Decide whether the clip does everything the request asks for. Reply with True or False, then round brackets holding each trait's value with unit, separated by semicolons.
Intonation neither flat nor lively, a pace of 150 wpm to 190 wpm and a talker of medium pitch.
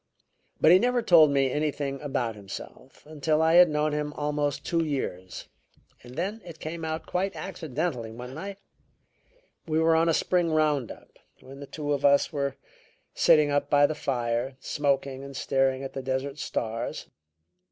True (3.0 semitones; 170 wpm; 145 Hz)